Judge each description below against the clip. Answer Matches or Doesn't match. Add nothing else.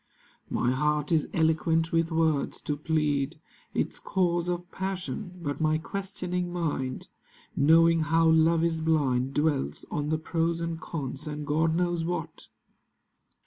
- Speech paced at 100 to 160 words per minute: Matches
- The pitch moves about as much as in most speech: Doesn't match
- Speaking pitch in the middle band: Matches